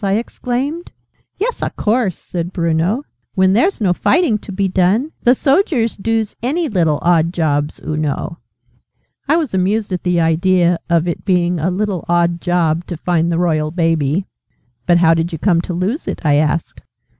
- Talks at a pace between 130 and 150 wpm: No, average, 180 wpm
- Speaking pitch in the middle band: Yes, medium, 180 Hz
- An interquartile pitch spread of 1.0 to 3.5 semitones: No, average, 4.4 semitones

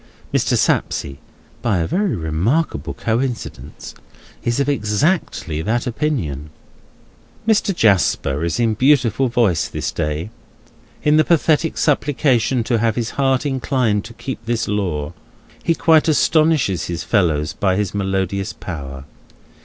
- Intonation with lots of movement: Yes, wide, 7.5 semitones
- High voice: No, low, 115 Hz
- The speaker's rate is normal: No, slow, 130 wpm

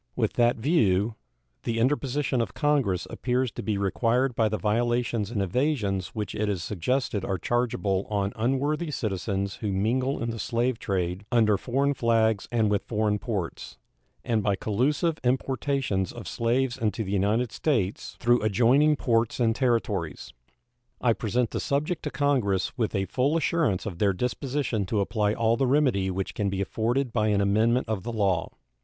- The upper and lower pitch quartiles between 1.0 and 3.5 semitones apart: No, average, 4.1 semitones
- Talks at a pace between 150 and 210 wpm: Yes, average, 170 wpm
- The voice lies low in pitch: Yes, low, 115 Hz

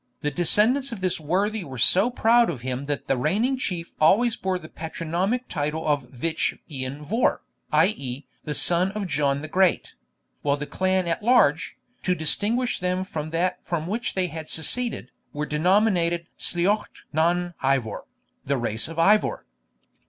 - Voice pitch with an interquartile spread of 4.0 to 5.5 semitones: Yes, average, 5.0 semitones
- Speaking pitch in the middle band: Yes, medium, 170 Hz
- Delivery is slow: No, average, 160 wpm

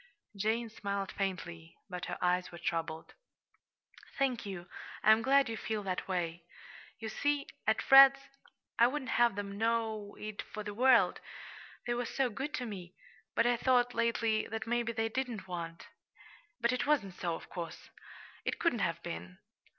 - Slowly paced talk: No, average, 165 wpm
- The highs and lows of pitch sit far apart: No, average, 4.5 semitones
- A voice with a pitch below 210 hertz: No, high, 220 Hz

